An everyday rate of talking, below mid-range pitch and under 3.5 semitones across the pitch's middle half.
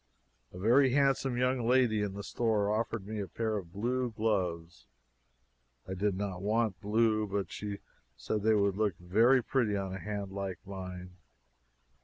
Yes: average, 165 wpm; low, 105 Hz; average, 3.0 semitones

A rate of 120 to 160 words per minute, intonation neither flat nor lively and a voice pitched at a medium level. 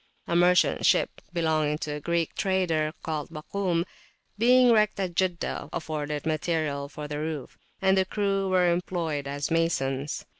Yes: average, 155 wpm; average, 3.7 semitones; medium, 165 Hz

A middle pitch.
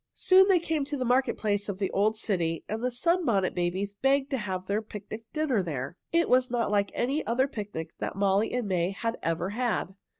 No: high, 215 Hz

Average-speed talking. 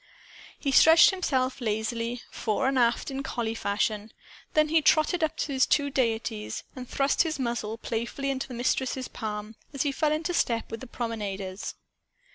Yes: average, 170 wpm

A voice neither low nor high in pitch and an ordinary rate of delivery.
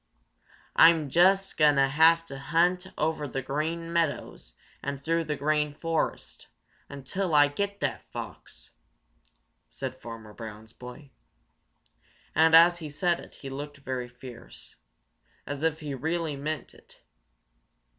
No: medium, 150 Hz; slow, 125 wpm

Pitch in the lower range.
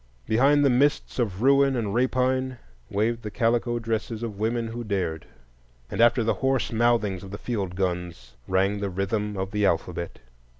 Yes: low, 110 Hz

